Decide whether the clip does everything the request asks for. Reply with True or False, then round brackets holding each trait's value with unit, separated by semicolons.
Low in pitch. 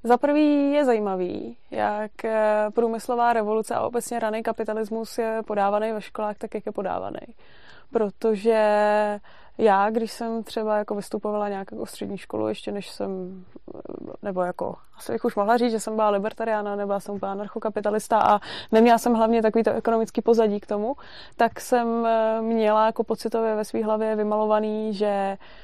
False (220 Hz)